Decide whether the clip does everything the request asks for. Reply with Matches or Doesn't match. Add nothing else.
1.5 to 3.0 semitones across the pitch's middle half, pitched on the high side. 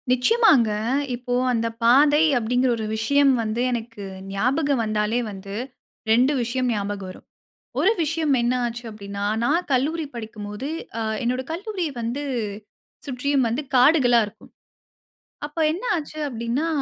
Doesn't match